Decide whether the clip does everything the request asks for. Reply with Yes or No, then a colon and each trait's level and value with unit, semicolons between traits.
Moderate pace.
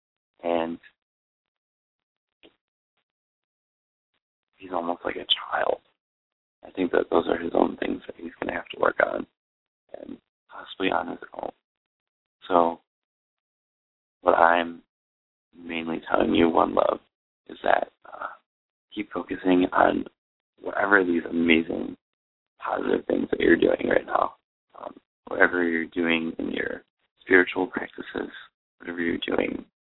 No: slow, 125 wpm